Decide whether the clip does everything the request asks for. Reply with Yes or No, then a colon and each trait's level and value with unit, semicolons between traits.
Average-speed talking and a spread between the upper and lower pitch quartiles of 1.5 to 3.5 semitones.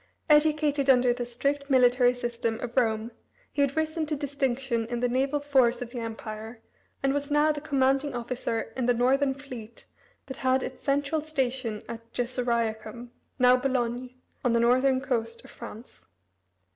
Yes: average, 160 wpm; average, 2.8 semitones